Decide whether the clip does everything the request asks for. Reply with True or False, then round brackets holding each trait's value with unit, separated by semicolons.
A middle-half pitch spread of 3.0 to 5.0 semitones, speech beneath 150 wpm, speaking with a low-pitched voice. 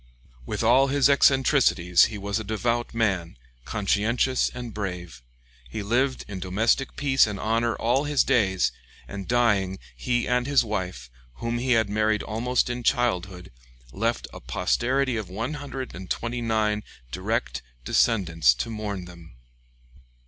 True (4.4 semitones; 135 wpm; 110 Hz)